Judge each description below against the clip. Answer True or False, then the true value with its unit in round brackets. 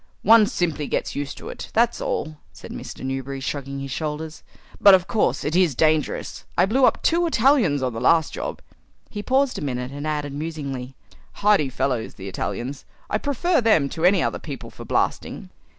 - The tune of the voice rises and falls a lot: True (7.1 semitones)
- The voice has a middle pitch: True (155 Hz)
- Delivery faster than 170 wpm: True (180 wpm)